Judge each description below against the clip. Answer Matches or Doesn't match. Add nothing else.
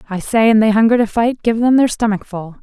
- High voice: Matches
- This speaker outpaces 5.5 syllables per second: Matches